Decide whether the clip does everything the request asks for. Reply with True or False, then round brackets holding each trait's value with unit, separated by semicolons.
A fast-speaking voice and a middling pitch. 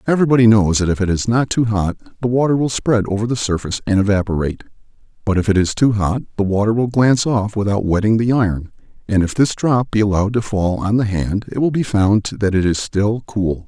False (235 wpm; 105 Hz)